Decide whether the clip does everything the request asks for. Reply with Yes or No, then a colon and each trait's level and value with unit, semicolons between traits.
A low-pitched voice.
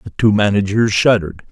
Yes: low, 100 Hz